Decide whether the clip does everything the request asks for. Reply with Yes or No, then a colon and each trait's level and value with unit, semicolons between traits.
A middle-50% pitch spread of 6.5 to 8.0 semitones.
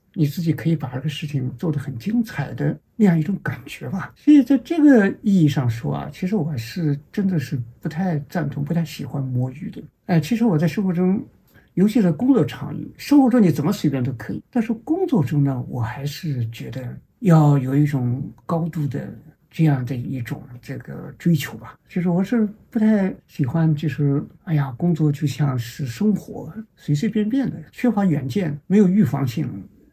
No: wide, 5.9 semitones